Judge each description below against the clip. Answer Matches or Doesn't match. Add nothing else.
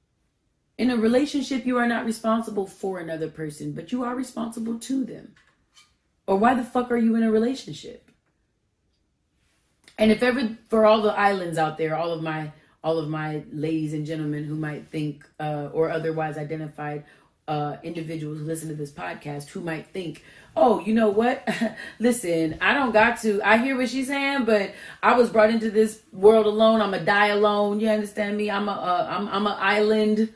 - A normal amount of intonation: Doesn't match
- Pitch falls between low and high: Doesn't match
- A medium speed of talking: Matches